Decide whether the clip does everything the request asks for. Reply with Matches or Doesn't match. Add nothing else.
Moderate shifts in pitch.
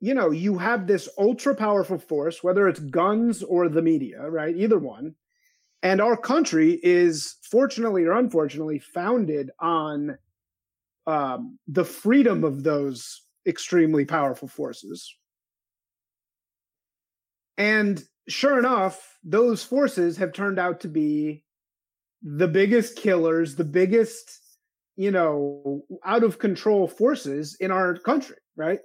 Doesn't match